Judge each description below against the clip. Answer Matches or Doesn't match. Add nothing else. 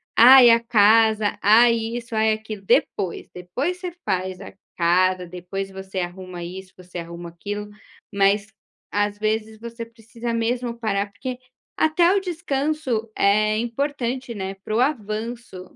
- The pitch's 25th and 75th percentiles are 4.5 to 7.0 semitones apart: Doesn't match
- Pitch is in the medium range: Doesn't match